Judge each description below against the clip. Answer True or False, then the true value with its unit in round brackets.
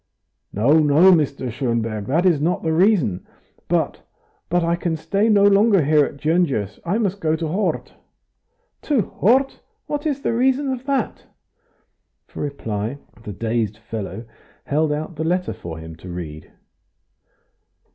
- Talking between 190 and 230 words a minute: False (150 wpm)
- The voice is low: False (155 Hz)